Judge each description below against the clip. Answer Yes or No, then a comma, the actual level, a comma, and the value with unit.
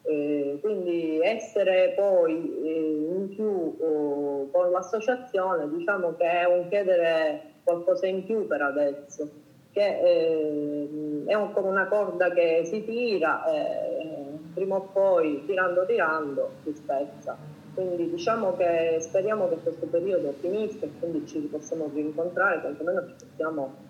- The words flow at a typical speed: Yes, average, 130 wpm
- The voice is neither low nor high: Yes, medium, 175 Hz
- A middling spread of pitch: Yes, average, 4.1 semitones